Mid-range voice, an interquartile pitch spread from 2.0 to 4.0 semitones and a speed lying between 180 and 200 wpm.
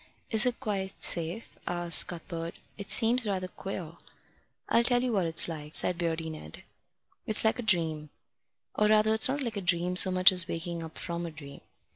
No: medium, 180 Hz; average, 4.5 semitones; average, 190 wpm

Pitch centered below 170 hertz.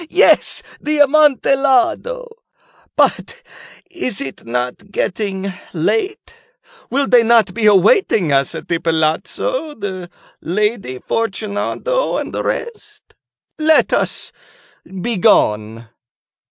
No: high, 220 Hz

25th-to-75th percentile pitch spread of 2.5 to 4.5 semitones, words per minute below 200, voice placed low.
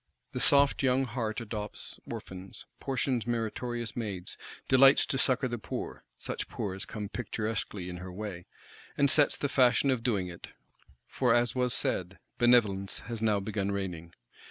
Yes: average, 4.2 semitones; average, 155 wpm; low, 110 Hz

